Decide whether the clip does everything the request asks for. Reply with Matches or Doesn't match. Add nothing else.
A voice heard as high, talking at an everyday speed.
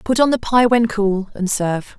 Doesn't match